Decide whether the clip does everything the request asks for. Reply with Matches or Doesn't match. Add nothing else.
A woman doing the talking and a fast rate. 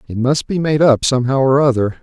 Doesn't match